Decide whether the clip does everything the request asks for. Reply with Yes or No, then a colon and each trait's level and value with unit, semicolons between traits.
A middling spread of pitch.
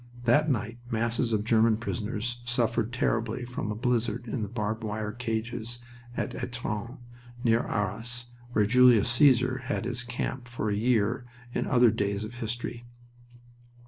No: narrow, 2.0 semitones